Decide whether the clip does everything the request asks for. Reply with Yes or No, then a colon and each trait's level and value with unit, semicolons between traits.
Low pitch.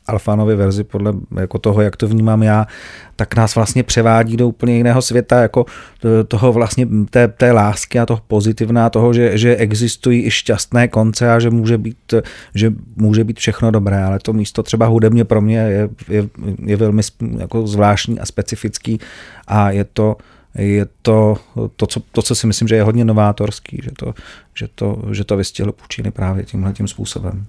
Yes: low, 110 Hz